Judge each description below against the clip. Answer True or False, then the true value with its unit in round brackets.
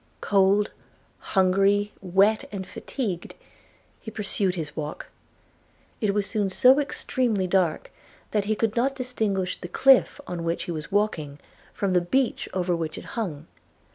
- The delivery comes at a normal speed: True (145 wpm)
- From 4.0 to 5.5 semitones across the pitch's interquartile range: False (3.4 semitones)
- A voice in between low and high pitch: False (195 Hz)